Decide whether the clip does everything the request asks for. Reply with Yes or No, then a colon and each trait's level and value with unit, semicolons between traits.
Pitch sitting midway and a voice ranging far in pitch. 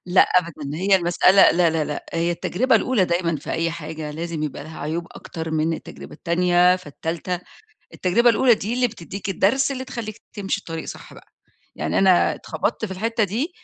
No: medium, 180 Hz; average, 4.0 semitones